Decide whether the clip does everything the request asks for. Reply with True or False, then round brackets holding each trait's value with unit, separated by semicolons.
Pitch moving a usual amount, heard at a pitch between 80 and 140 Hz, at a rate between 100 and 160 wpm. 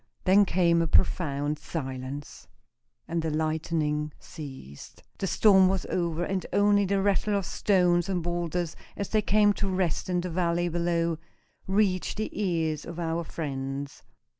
False (3.4 semitones; 170 Hz; 150 wpm)